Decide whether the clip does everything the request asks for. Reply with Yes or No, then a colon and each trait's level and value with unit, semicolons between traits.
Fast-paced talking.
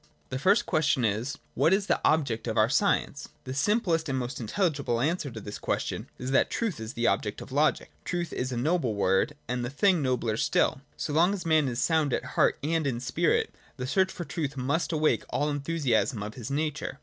Yes: fast, 220 wpm